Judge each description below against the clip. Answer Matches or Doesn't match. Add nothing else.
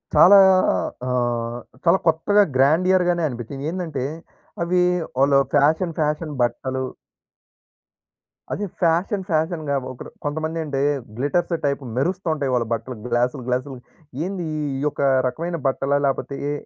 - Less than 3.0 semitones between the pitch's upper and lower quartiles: Doesn't match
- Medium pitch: Matches